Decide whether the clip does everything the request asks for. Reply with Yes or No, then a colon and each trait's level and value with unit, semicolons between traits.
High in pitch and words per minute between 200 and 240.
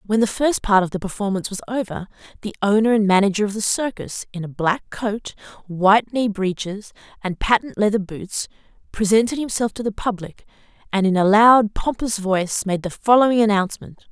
No: high, 210 Hz; average, 180 wpm